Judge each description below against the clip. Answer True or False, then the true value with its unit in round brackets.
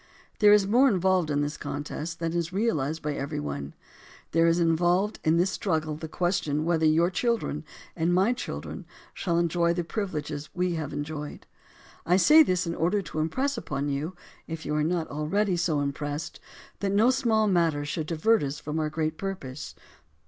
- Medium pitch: True (165 Hz)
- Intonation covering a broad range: False (3.9 semitones)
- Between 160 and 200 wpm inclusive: True (180 wpm)